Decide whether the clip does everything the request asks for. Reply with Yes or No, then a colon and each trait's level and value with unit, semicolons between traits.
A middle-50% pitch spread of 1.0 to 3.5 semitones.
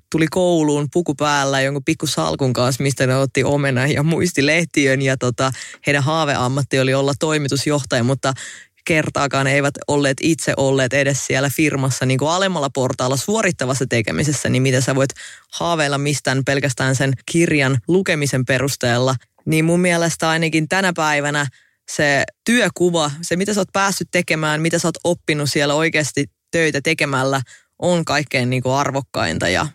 Yes: average, 3.2 semitones